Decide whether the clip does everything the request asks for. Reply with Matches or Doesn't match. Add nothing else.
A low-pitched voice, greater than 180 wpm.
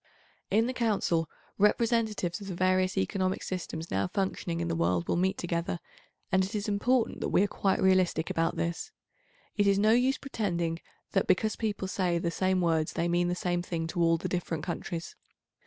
Doesn't match